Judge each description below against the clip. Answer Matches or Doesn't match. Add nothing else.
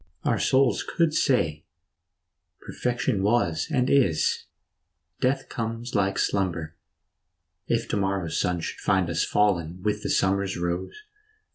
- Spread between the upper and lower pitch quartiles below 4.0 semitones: Doesn't match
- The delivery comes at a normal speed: Doesn't match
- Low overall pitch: Matches